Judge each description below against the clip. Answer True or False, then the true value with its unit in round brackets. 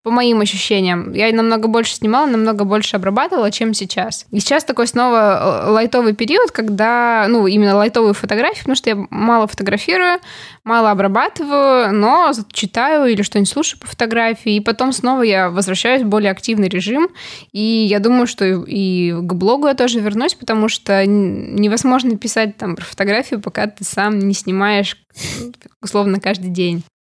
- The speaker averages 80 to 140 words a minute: False (160 wpm)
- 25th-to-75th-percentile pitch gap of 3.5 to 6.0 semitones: False (3.0 semitones)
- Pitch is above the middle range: True (220 Hz)